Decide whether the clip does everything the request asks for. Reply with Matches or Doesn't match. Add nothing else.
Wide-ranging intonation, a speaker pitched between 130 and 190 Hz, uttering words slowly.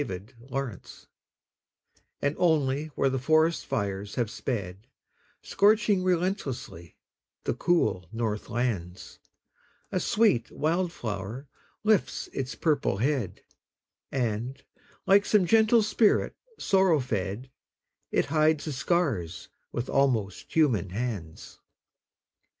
Matches